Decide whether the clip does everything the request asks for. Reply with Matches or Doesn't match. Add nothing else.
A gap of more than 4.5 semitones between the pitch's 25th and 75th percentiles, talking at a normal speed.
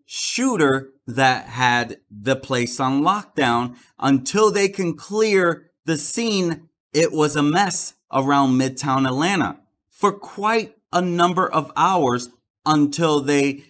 Doesn't match